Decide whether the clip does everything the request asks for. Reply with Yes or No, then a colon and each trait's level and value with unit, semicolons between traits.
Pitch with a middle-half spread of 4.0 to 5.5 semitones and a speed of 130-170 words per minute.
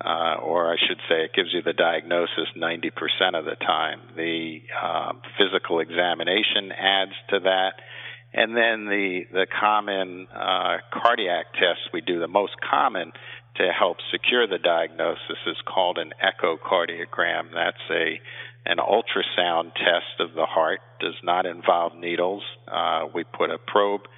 No: average, 2.7 semitones; average, 150 wpm